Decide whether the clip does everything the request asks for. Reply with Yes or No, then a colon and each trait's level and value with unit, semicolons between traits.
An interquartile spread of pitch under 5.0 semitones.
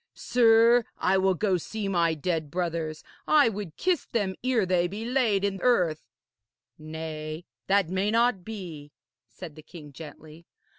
No: wide, 5.5 semitones